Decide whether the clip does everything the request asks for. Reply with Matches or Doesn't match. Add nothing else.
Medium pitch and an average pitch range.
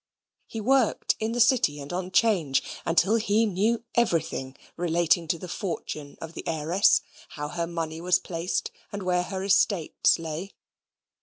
Matches